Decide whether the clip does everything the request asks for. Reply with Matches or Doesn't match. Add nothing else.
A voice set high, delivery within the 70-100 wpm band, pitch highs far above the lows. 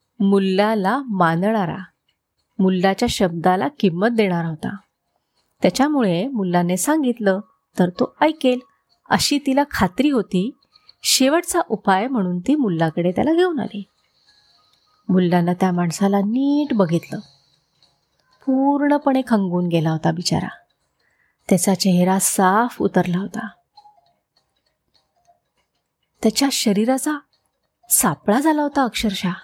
Matches